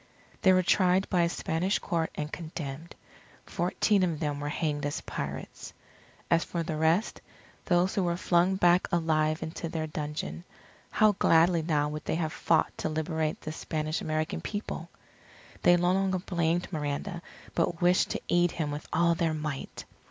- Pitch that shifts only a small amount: Yes, narrow, 2.3 semitones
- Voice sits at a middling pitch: Yes, medium, 165 Hz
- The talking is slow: No, average, 165 wpm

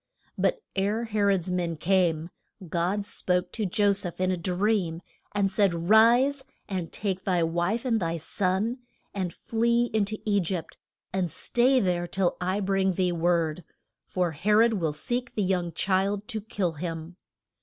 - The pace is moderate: Yes, average, 170 wpm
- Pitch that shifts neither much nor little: Yes, average, 3.4 semitones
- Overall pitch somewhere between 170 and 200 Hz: Yes, high, 190 Hz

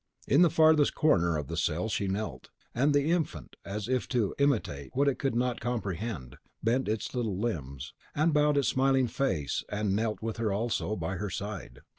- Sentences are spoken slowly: No, average, 190 wpm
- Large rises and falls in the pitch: Yes, wide, 6.3 semitones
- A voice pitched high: No, low, 110 Hz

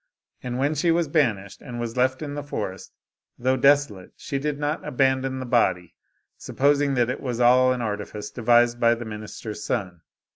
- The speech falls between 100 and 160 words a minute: No, average, 185 wpm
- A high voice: No, low, 125 Hz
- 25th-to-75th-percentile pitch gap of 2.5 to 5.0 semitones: Yes, average, 3.5 semitones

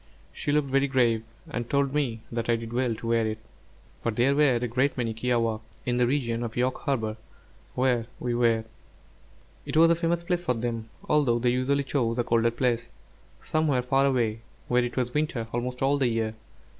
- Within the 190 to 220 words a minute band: Yes, average, 195 wpm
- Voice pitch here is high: No, low, 125 Hz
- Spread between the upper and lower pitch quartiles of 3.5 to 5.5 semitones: No, average, 2.9 semitones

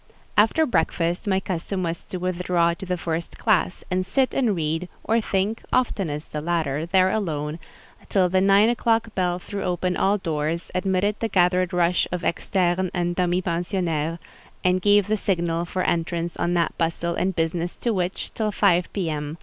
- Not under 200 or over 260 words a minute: No, average, 175 wpm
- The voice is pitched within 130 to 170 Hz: No, medium, 180 Hz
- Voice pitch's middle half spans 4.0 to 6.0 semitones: No, narrow, 2.4 semitones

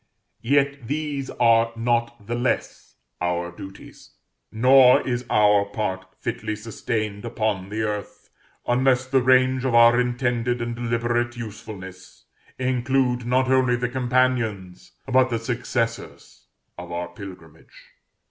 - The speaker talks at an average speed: No, slow, 120 wpm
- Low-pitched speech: Yes, low, 120 Hz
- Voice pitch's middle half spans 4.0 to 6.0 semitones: No, average, 3.1 semitones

